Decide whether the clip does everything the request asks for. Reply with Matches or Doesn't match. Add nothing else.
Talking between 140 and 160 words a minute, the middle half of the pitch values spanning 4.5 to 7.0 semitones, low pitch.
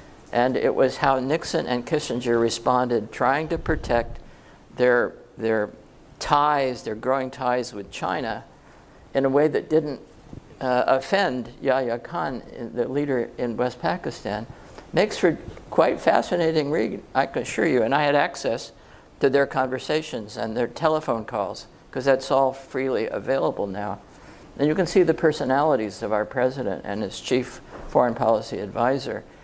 Doesn't match